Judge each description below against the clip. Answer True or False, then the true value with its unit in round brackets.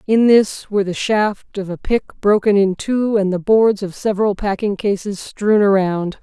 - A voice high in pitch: True (205 Hz)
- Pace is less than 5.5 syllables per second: True (4.4 syllables/s)